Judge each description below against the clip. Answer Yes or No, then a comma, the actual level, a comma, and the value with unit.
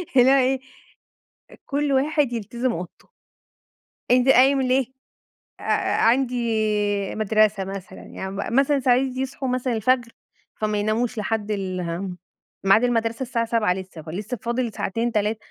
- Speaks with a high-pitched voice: Yes, high, 230 Hz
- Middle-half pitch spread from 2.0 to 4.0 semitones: Yes, average, 3.7 semitones